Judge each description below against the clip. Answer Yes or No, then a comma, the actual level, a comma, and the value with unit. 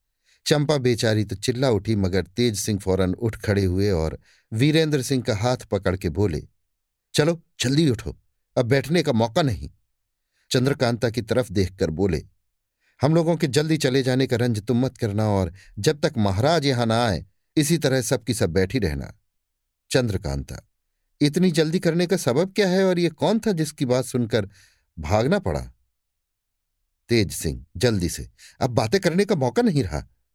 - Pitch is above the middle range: No, low, 120 Hz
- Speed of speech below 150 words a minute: No, average, 170 wpm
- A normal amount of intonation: No, wide, 7.0 semitones